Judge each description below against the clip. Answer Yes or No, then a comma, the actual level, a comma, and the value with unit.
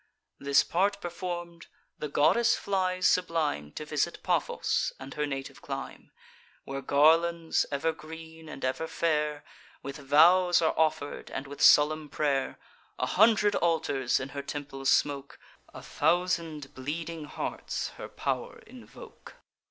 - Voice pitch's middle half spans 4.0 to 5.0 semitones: No, average, 3.3 semitones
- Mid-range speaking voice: Yes, medium, 155 Hz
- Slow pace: Yes, slow, 130 wpm